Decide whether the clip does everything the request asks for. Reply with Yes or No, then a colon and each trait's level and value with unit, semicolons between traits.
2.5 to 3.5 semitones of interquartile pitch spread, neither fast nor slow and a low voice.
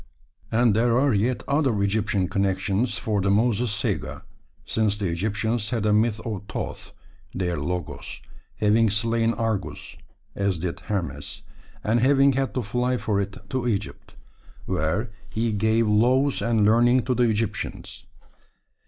Yes: average, 3.0 semitones; average, 145 wpm; low, 110 Hz